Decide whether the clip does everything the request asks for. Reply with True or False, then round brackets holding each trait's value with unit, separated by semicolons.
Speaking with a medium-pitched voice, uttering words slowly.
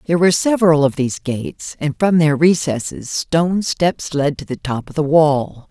False (155 Hz; 200 wpm)